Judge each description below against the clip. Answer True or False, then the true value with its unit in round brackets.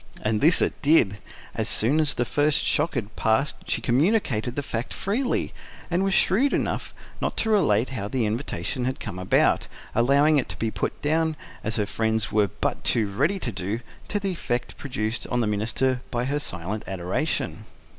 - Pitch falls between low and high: False (125 Hz)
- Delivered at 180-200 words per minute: True (185 wpm)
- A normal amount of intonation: False (5.8 semitones)